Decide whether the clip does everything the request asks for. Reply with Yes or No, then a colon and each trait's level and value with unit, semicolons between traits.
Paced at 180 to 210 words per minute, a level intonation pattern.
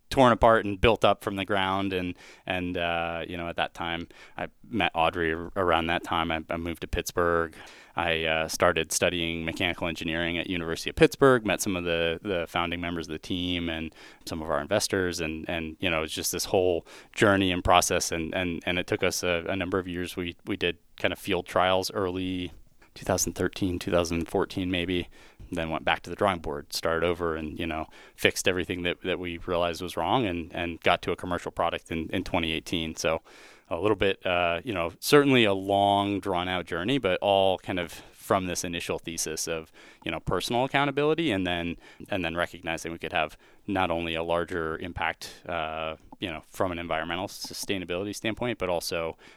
Yes: average, 200 wpm; narrow, 2.3 semitones